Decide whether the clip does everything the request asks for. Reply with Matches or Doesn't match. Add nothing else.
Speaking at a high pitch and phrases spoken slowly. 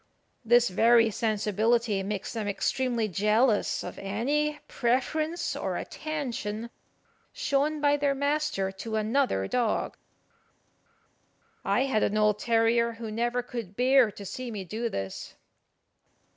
Matches